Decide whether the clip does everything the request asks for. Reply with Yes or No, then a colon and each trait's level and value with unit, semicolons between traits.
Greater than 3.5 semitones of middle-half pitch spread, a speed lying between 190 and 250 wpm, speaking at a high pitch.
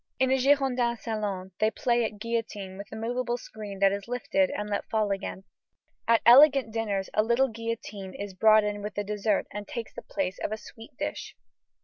No: average, 2.7 semitones; average, 200 wpm; high, 215 Hz